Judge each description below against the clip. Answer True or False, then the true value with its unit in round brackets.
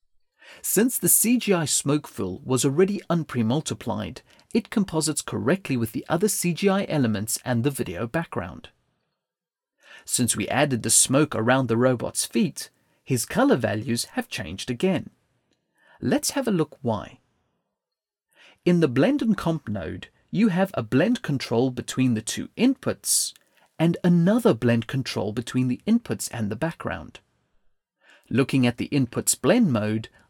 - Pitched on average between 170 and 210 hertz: False (135 Hz)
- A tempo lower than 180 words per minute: True (140 wpm)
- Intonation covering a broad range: True (7.3 semitones)